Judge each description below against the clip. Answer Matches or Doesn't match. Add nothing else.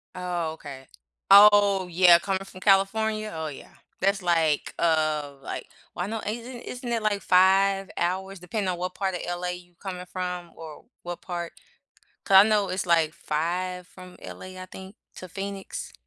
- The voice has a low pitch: Doesn't match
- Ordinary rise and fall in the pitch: Doesn't match